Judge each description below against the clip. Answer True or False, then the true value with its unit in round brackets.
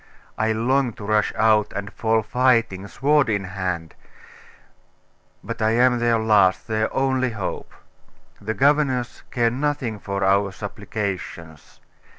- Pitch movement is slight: False (3.6 semitones)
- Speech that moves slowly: True (130 wpm)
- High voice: False (110 Hz)